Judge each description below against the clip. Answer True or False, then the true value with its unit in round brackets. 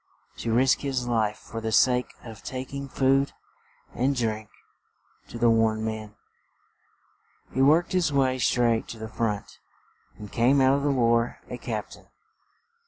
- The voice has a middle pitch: False (120 Hz)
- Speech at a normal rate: True (160 wpm)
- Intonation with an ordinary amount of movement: True (3.1 semitones)